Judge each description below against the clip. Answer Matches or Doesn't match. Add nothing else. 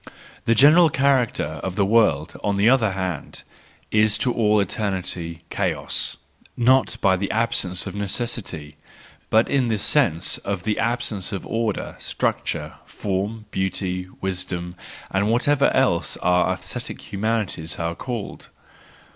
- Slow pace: Matches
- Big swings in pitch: Doesn't match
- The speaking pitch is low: Matches